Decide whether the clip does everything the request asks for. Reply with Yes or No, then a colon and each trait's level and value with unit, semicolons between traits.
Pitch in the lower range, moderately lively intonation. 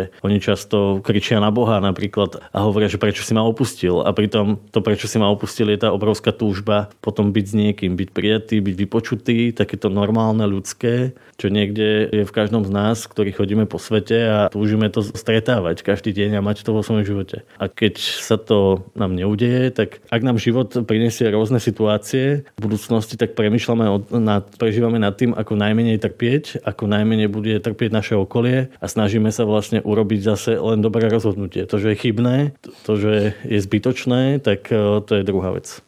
No: low, 110 Hz; narrow, 1.8 semitones